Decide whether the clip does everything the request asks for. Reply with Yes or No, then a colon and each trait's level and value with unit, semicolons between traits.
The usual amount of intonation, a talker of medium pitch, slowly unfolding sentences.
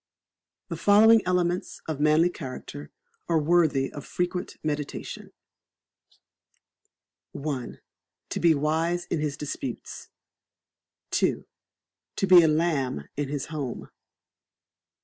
Yes: average, 3.3 semitones; medium, 155 Hz; slow, 105 wpm